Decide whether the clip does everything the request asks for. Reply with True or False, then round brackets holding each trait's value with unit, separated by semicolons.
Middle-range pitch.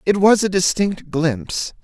True (175 Hz)